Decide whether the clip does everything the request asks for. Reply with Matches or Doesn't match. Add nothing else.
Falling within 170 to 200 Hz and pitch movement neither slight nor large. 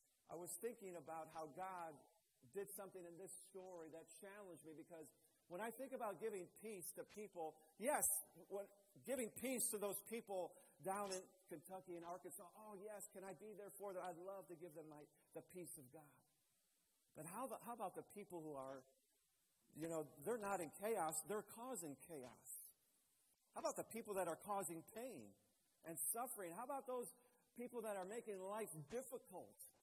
Matches